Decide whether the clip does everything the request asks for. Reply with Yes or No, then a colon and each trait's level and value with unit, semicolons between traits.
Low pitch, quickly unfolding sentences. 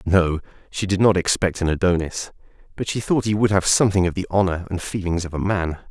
Yes: very low, 95 Hz; fast, 225 wpm